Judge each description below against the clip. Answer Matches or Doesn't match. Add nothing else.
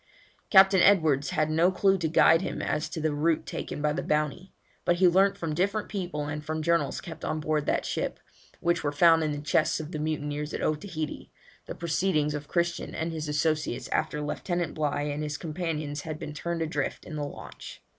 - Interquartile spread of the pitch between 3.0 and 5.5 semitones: Doesn't match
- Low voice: Doesn't match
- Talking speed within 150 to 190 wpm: Doesn't match